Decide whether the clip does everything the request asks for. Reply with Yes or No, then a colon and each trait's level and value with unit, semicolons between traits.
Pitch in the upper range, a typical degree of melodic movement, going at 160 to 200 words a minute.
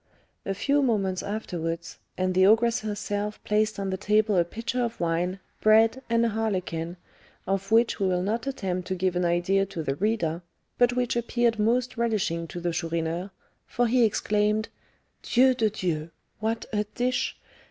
Yes: high, 210 Hz; average, 4.1 semitones; average, 170 wpm